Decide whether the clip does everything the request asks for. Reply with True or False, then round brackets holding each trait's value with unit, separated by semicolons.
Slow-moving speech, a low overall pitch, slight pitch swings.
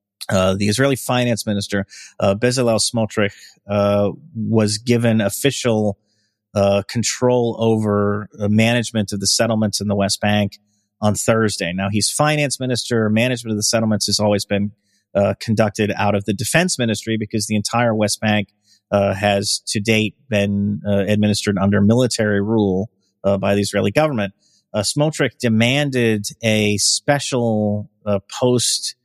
False (145 wpm; 105 Hz; 2.2 semitones)